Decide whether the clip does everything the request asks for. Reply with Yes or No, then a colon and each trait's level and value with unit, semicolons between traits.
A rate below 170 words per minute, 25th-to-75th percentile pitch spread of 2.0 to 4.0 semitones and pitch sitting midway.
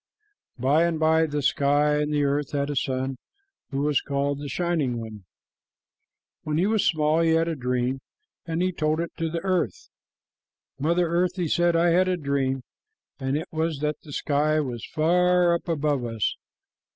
No: average, 180 wpm; average, 3.2 semitones; medium, 155 Hz